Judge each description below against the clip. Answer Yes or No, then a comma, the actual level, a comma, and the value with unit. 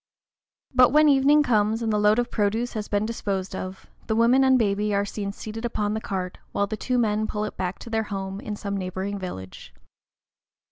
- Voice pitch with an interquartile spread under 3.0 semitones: Yes, narrow, 2.6 semitones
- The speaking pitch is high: Yes, high, 210 Hz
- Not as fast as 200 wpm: No, fast, 205 wpm